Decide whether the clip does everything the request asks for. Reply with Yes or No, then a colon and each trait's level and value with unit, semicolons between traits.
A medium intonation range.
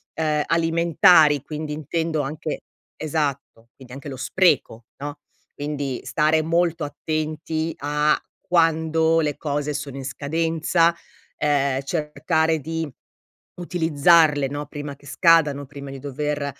No: narrow, 2.2 semitones